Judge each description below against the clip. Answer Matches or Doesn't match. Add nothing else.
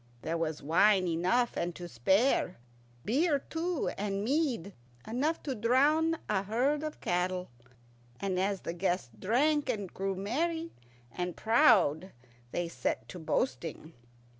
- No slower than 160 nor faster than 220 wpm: Doesn't match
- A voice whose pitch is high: Matches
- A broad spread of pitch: Matches